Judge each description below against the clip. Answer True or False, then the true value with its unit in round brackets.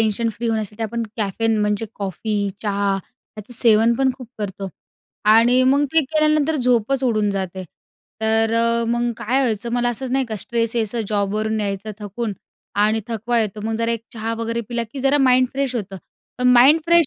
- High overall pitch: True (230 Hz)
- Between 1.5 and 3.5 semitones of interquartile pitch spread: True (2.9 semitones)